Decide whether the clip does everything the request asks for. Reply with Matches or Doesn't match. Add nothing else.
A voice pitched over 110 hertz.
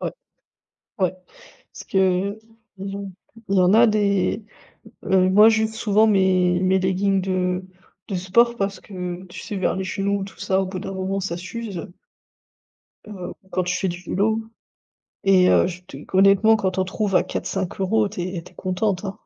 Matches